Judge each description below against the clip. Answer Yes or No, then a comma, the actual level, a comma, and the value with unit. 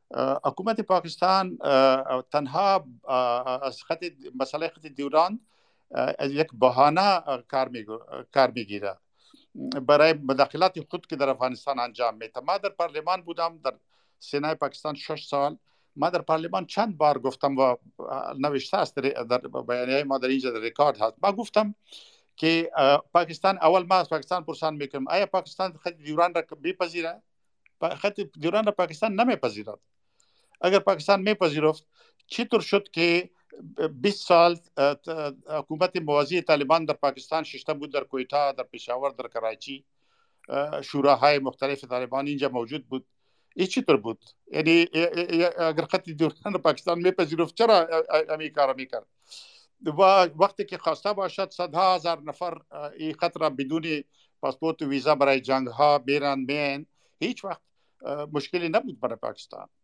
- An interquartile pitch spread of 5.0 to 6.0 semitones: No, average, 4.6 semitones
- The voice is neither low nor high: Yes, medium, 155 Hz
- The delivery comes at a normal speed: Yes, average, 130 wpm